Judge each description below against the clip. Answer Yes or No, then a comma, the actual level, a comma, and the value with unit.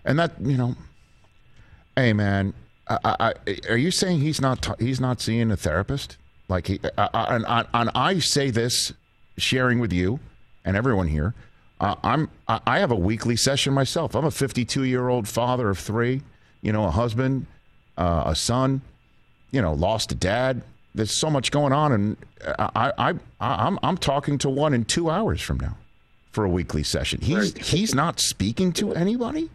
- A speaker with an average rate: Yes, average, 190 wpm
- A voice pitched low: Yes, low, 125 Hz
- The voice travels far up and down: No, average, 4.5 semitones